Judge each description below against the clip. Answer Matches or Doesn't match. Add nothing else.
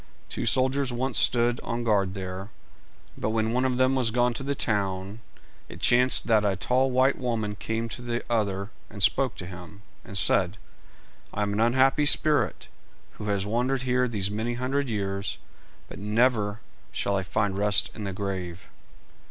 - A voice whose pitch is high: Doesn't match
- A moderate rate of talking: Matches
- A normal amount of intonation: Matches